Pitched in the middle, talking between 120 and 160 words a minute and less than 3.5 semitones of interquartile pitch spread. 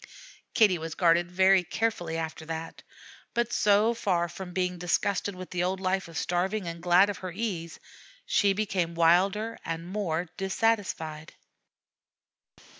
Yes: medium, 180 Hz; average, 140 wpm; average, 2.9 semitones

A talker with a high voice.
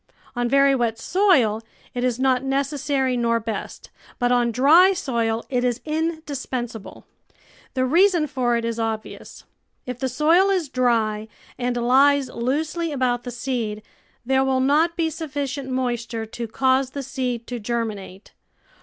Yes: very high, 255 Hz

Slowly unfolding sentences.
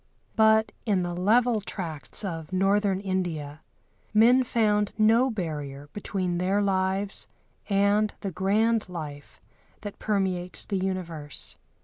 Yes: slow, 115 wpm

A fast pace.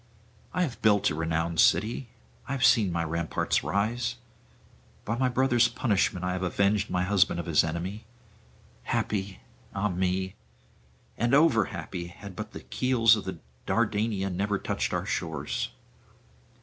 No: average, 145 wpm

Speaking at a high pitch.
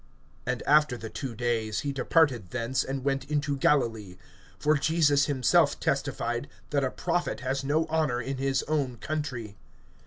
No: low, 135 Hz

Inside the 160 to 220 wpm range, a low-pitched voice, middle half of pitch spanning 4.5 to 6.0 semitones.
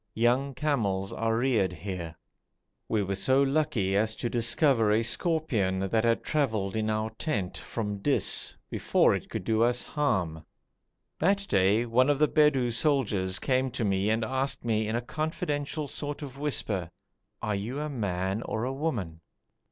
Yes: average, 165 wpm; low, 115 Hz; wide, 5.5 semitones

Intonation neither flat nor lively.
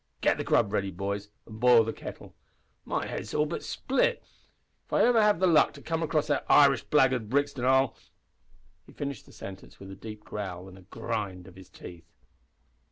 No: wide, 6.6 semitones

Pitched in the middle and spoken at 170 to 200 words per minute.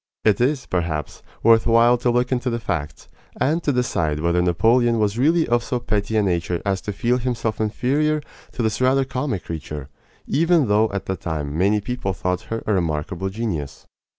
No: low, 110 Hz; average, 185 wpm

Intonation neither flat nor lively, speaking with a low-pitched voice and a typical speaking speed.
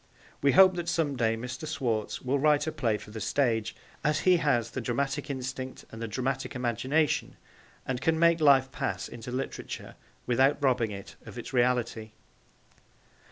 Yes: average, 3.8 semitones; low, 130 Hz; average, 165 wpm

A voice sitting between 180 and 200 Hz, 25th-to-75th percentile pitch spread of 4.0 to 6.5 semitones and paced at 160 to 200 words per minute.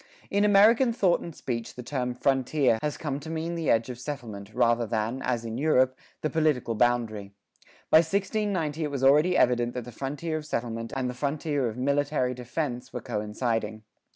No: low, 130 Hz; average, 4.7 semitones; average, 180 wpm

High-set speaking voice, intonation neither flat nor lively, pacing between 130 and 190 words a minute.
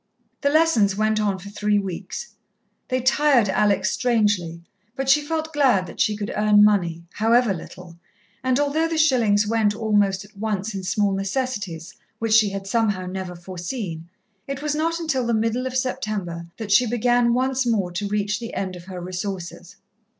Yes: high, 210 Hz; average, 4.7 semitones; average, 175 wpm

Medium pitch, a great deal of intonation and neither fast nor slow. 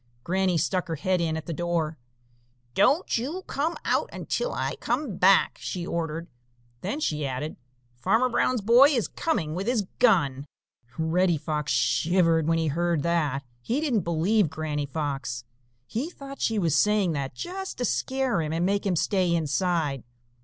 Yes: medium, 175 Hz; wide, 6.2 semitones; average, 165 wpm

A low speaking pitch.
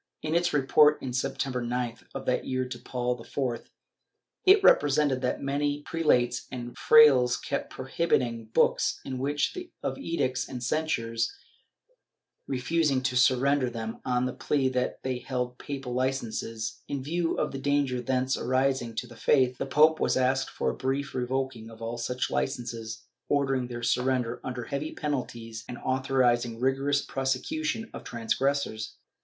Yes: low, 130 Hz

